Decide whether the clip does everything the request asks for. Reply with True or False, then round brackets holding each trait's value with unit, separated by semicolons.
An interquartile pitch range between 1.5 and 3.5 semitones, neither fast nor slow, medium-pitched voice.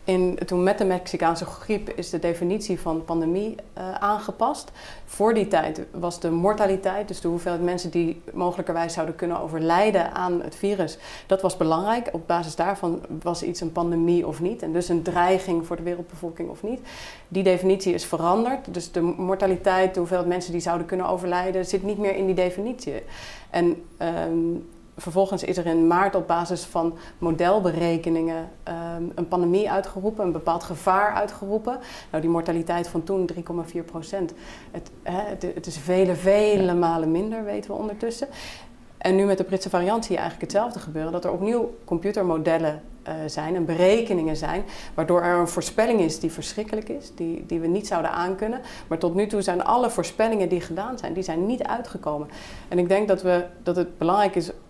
True (2.5 semitones; 180 wpm; 180 Hz)